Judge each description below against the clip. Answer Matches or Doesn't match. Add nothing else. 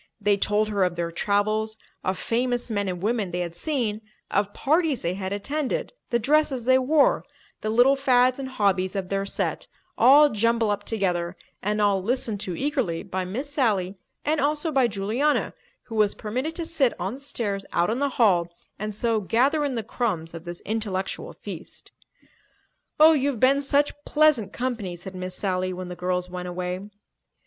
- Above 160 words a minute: Matches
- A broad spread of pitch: Matches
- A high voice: Matches